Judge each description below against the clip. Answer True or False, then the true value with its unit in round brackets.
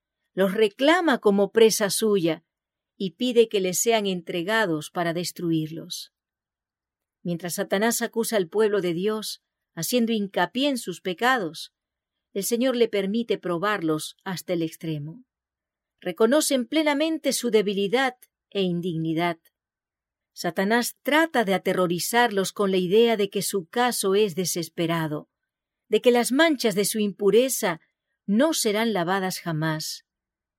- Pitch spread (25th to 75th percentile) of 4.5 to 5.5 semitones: True (4.8 semitones)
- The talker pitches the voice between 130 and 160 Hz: False (205 Hz)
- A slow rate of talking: True (125 wpm)